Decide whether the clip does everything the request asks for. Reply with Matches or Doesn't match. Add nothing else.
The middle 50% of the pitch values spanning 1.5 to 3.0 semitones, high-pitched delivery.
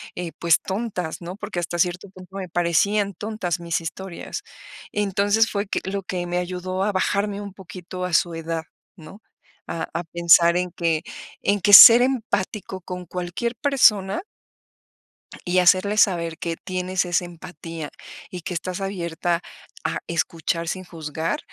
Doesn't match